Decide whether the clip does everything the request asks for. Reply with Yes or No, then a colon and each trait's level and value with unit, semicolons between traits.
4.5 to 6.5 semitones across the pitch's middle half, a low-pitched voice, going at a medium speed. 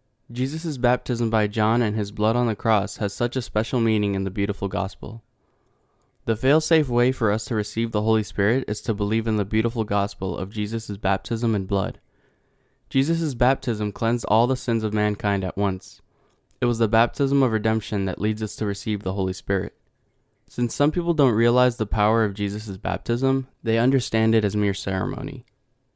No: average, 3.5 semitones; low, 110 Hz; average, 185 wpm